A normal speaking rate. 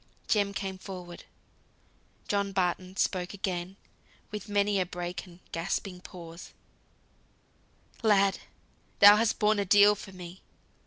No: slow, 120 wpm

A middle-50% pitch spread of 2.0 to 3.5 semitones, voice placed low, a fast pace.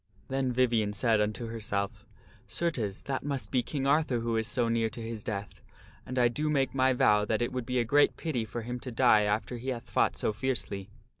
Yes: average, 3.2 semitones; low, 120 Hz; fast, 225 wpm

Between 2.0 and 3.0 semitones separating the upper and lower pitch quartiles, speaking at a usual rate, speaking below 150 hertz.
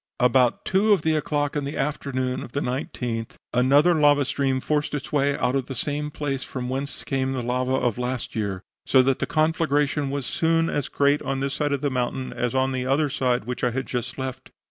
No: narrow, 2.4 semitones; fast, 210 wpm; low, 135 Hz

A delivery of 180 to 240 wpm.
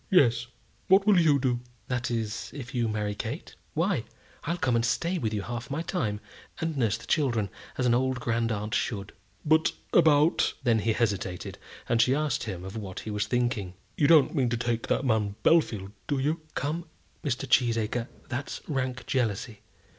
Yes: average, 185 wpm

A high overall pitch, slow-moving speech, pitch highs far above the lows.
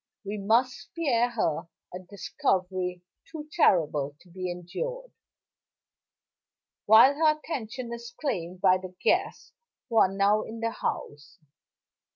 Yes: high, 210 Hz; slow, 125 wpm; wide, 5.7 semitones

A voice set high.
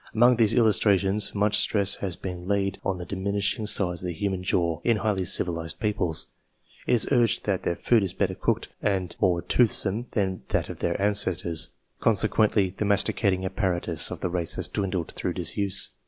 No: low, 100 Hz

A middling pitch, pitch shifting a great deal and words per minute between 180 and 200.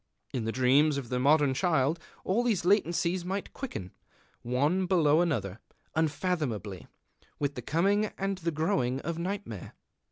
No: medium, 155 Hz; wide, 6.1 semitones; average, 140 wpm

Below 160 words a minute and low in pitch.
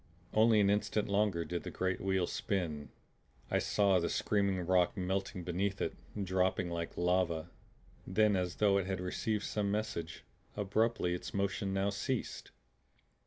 Yes: average, 150 wpm; very low, 95 Hz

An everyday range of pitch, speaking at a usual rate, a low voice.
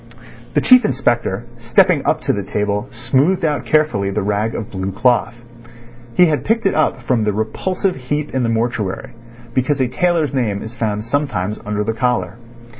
No: wide, 5.8 semitones; average, 180 wpm; low, 120 Hz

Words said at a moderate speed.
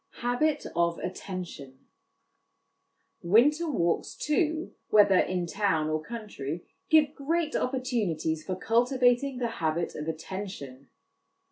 No: slow, 105 wpm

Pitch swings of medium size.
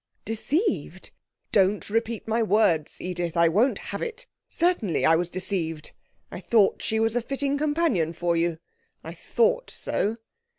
No: wide, 8.0 semitones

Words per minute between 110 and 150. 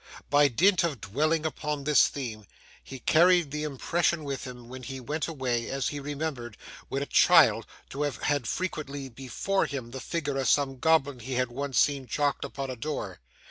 No: average, 185 wpm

